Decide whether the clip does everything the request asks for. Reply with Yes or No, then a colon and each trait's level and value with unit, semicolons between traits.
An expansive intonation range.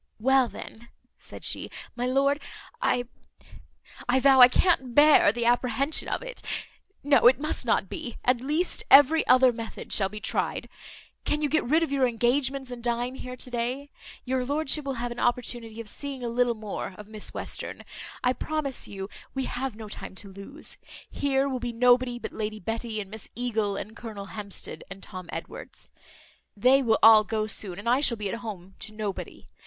No: average, 3.5 semitones